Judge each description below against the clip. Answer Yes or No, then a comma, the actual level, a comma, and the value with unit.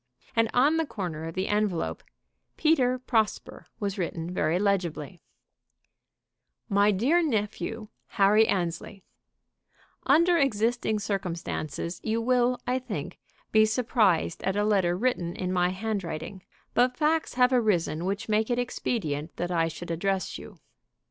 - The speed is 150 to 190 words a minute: No, slow, 135 wpm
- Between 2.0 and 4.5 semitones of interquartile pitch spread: No, wide, 5.4 semitones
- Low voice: No, high, 205 Hz